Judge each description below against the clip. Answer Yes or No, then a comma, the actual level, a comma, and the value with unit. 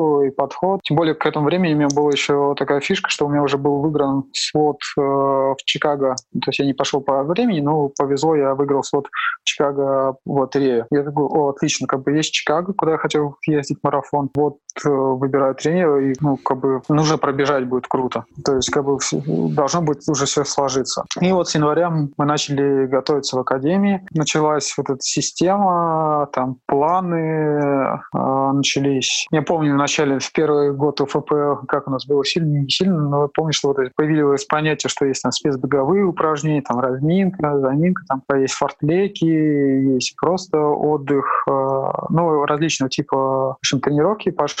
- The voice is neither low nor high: Yes, medium, 145 Hz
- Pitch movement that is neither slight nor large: No, narrow, 2.1 semitones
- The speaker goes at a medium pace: No, fast, 180 wpm